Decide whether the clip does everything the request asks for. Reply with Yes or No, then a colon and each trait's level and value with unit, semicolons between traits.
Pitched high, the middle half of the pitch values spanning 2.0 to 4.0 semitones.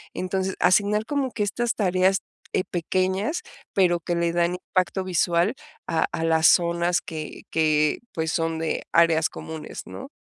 No: medium, 175 Hz; average, 2.8 semitones